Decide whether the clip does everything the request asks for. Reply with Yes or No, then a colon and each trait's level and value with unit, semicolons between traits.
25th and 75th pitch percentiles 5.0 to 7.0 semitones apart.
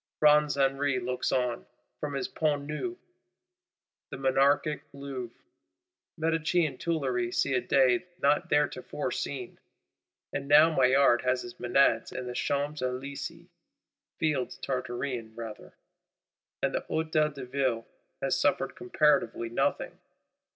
No: average, 2.9 semitones